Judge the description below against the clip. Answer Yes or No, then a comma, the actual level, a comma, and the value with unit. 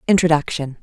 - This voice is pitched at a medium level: Yes, medium, 160 Hz